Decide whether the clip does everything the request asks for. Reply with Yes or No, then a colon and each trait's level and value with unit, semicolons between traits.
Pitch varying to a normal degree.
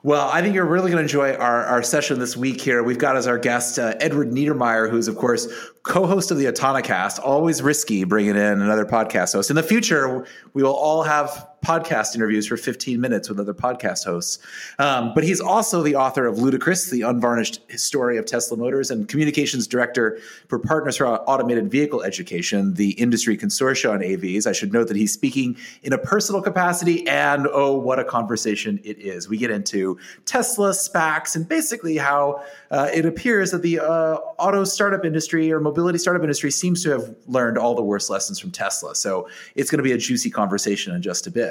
No: wide, 6.0 semitones